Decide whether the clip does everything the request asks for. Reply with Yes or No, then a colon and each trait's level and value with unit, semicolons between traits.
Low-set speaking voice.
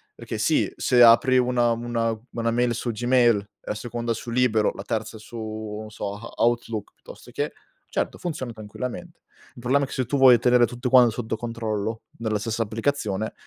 Yes: low, 115 Hz